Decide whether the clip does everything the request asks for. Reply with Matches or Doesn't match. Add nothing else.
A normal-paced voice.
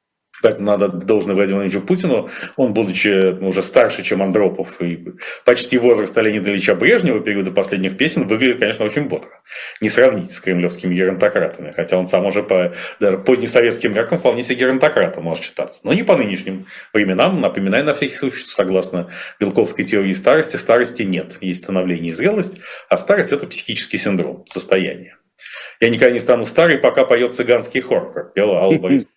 Doesn't match